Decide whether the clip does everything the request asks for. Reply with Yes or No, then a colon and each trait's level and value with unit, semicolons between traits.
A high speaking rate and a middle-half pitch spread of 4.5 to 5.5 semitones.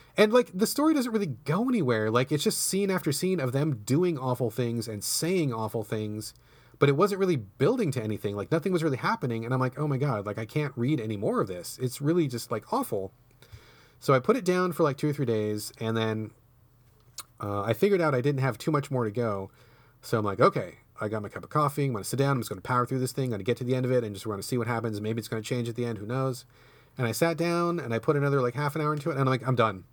Yes: fast, 295 wpm; average, 4.8 semitones